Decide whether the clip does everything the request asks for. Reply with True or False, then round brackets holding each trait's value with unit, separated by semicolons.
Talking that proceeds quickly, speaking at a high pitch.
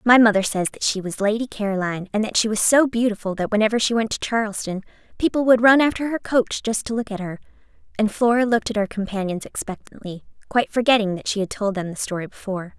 True (225 wpm; 215 Hz)